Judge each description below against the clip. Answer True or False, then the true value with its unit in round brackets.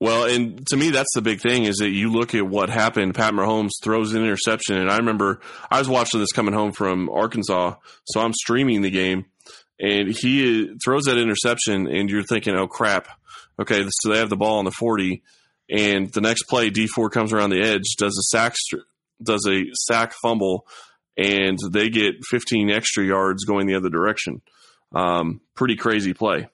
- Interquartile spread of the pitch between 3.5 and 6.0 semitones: False (2.8 semitones)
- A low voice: True (105 Hz)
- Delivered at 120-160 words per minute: False (190 wpm)